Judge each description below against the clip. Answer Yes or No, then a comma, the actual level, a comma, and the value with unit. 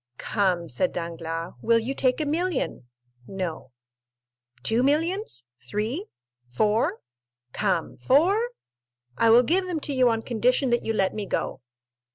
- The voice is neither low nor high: No, high, 225 Hz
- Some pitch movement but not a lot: No, wide, 8.5 semitones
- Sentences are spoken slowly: Yes, slow, 130 wpm